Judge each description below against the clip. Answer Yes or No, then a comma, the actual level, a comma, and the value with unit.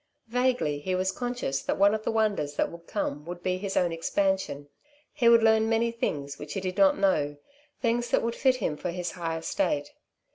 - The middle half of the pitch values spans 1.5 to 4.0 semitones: No, wide, 5.6 semitones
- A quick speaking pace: Yes, fast, 210 wpm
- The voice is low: No, high, 190 Hz